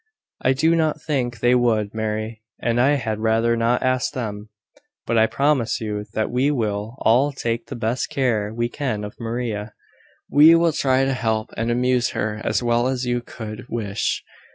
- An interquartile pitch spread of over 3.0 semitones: No, average, 2.7 semitones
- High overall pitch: No, low, 120 Hz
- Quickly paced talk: No, average, 180 wpm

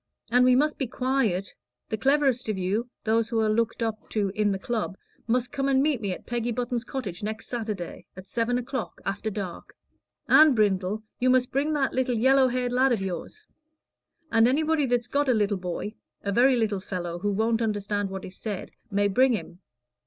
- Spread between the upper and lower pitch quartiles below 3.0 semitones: No, average, 3.9 semitones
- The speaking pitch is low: No, high, 230 Hz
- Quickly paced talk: No, average, 195 wpm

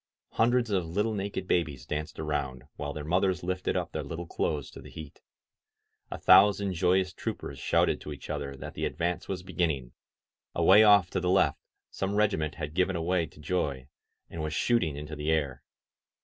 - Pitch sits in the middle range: No, very low, 85 Hz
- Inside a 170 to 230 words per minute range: Yes, average, 180 wpm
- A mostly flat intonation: No, average, 4.2 semitones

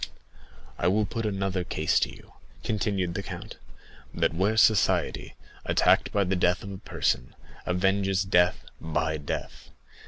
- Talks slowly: No, average, 145 wpm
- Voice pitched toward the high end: No, very low, 95 Hz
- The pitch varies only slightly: Yes, narrow, 2.1 semitones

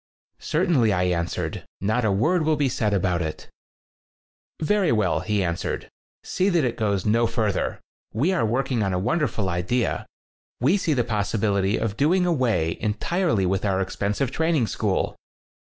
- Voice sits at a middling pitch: No, low, 110 Hz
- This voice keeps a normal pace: Yes, average, 160 wpm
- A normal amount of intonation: No, wide, 7.1 semitones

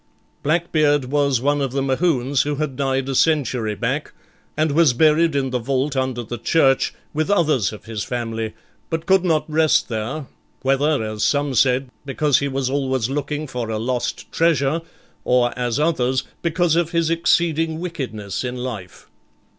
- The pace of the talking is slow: No, average, 165 wpm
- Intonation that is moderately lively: Yes, average, 3.9 semitones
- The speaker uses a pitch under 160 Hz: Yes, low, 135 Hz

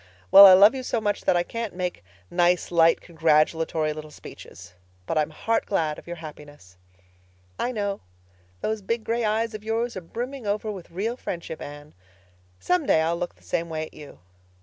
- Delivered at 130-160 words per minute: No, average, 190 wpm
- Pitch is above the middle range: No, medium, 175 Hz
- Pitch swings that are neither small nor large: No, wide, 5.7 semitones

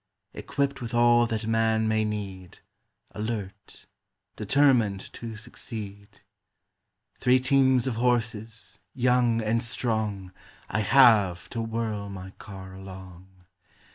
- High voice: No, low, 110 Hz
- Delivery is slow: Yes, slow, 110 wpm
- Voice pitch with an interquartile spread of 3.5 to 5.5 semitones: No, average, 3.1 semitones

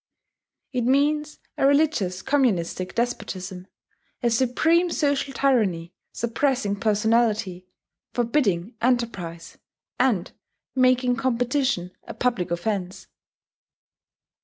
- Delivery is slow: Yes, slow, 85 wpm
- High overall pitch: Yes, high, 235 Hz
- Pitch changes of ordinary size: No, wide, 6.1 semitones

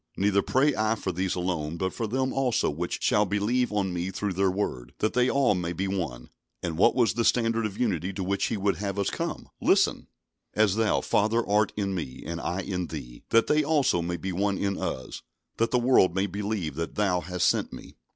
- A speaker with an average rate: No, fast, 220 wpm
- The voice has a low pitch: Yes, low, 100 Hz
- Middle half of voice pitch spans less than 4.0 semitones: Yes, average, 3.6 semitones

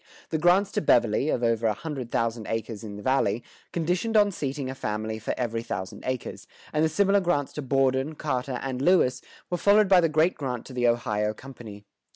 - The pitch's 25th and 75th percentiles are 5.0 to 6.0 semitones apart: Yes, wide, 5.6 semitones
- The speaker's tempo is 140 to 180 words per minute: No, average, 200 wpm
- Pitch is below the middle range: Yes, low, 130 Hz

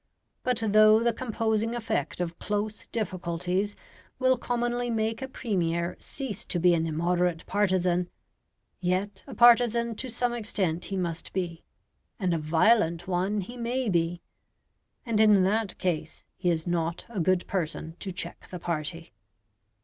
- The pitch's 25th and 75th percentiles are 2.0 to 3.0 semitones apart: No, average, 4.6 semitones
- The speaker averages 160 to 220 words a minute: No, average, 150 wpm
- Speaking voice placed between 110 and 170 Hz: No, high, 195 Hz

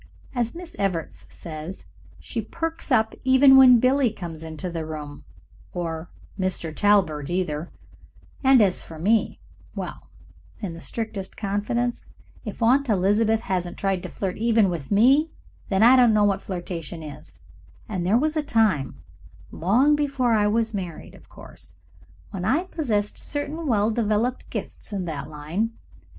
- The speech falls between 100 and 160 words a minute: Yes, average, 150 wpm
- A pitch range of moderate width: No, wide, 5.7 semitones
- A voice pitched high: Yes, high, 205 Hz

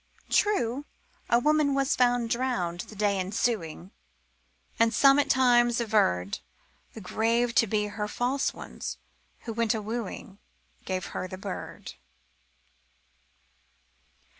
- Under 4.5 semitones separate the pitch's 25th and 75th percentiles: Yes, average, 3.3 semitones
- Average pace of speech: No, slow, 115 wpm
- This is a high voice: Yes, high, 230 Hz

